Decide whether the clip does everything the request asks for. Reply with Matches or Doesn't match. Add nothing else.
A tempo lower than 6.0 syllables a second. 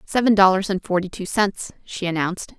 Matches